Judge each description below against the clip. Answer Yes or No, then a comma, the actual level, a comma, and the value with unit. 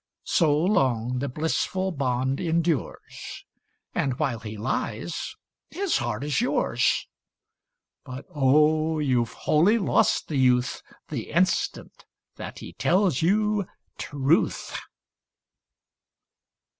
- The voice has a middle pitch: Yes, medium, 150 Hz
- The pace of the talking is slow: Yes, slow, 105 wpm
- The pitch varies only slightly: No, average, 5.3 semitones